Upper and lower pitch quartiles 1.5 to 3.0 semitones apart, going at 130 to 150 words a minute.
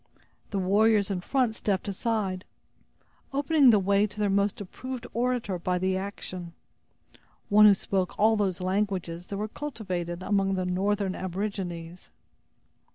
Yes: narrow, 2.4 semitones; average, 140 wpm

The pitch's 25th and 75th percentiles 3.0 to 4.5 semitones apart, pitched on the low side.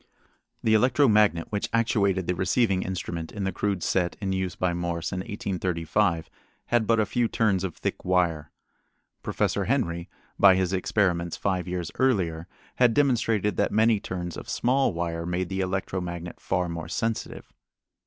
Yes: average, 3.6 semitones; very low, 95 Hz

